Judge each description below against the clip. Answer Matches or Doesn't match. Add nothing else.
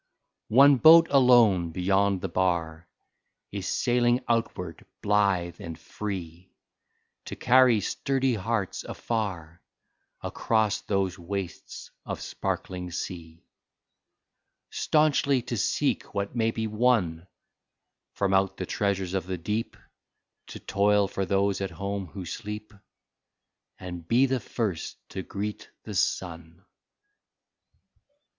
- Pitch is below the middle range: Matches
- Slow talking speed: Matches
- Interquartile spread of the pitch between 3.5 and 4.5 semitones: Matches